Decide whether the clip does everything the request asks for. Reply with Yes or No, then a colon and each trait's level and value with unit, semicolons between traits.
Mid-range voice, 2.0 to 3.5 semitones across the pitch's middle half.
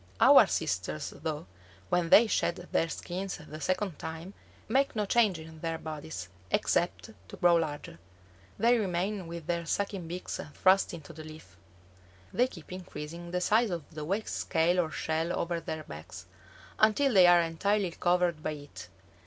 Yes: medium, 170 Hz; average, 3.2 semitones